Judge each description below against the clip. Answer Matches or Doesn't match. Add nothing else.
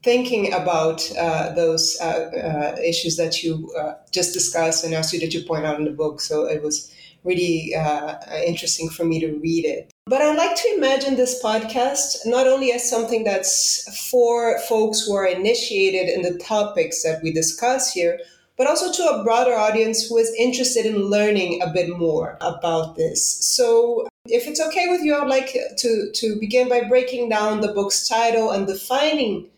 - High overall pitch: Matches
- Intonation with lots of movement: Matches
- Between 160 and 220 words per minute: Matches